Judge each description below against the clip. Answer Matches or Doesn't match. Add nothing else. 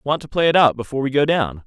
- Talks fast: Matches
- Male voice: Matches